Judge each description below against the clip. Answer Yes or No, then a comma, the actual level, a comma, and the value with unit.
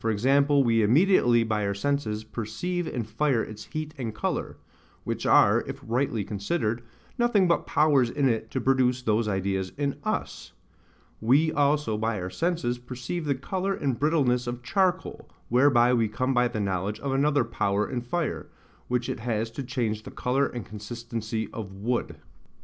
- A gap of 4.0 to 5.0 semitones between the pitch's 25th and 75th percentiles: Yes, average, 4.5 semitones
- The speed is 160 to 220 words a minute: Yes, average, 165 wpm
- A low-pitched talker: Yes, low, 120 Hz